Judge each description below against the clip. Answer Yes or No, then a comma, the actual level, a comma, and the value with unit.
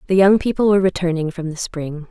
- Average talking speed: No, fast, 230 wpm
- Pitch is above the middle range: No, medium, 175 Hz